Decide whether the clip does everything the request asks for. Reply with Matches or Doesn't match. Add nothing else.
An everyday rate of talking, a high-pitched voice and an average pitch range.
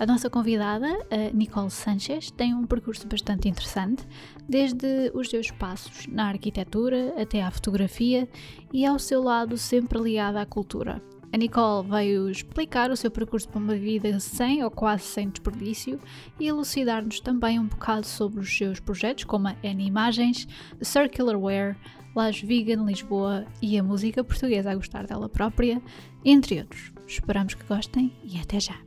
Matches